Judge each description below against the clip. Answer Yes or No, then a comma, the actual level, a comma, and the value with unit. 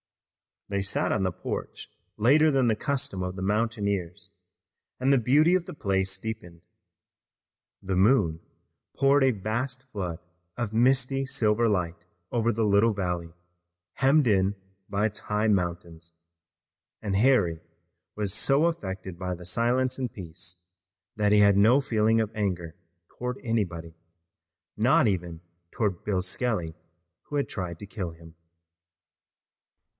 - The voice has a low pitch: Yes, low, 105 Hz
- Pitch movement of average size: Yes, average, 5.0 semitones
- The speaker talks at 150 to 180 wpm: No, average, 140 wpm